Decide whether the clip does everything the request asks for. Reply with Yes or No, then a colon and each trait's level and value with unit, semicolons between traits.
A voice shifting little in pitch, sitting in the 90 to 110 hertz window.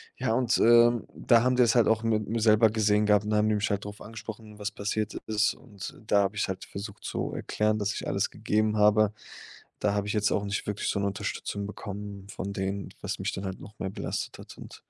Yes: narrow, 1.3 semitones; low, 105 Hz